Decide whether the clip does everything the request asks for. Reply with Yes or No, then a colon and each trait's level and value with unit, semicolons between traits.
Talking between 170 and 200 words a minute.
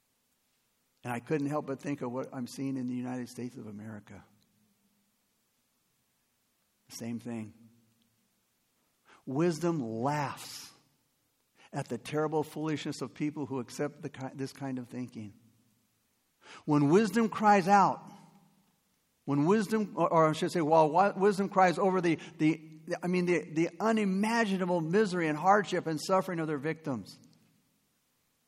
No: slow, 135 wpm